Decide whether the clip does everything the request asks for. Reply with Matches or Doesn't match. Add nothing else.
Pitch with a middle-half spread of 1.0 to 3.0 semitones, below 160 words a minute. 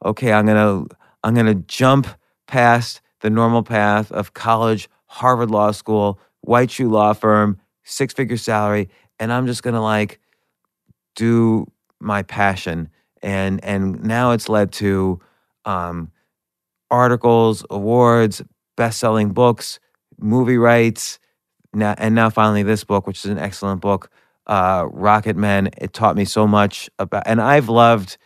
Matches